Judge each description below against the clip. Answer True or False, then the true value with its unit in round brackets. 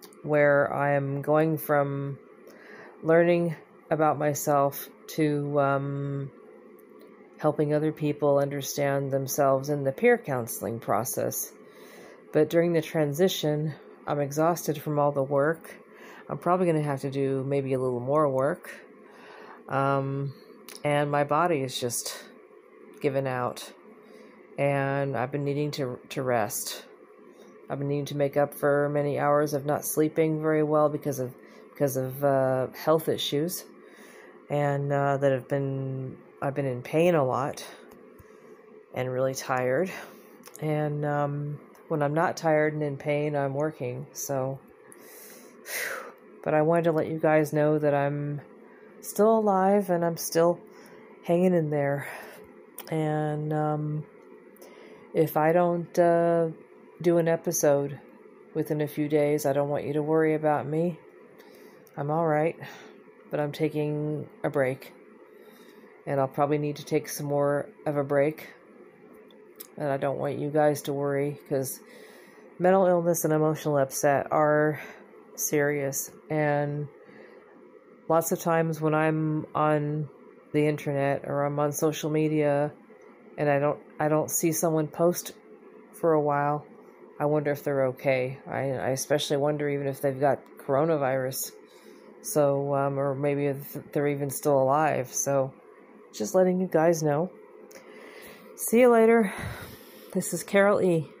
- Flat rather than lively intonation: True (1.9 semitones)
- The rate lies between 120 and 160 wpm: True (140 wpm)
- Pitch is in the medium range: True (145 Hz)